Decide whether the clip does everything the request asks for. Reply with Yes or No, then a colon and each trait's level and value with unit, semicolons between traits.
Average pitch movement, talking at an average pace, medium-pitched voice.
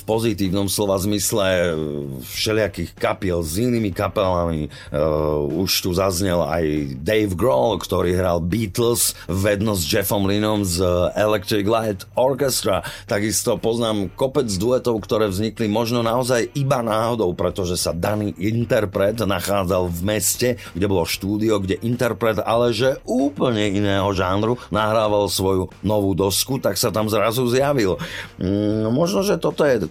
No: average, 3.2 semitones; average, 135 wpm; low, 105 Hz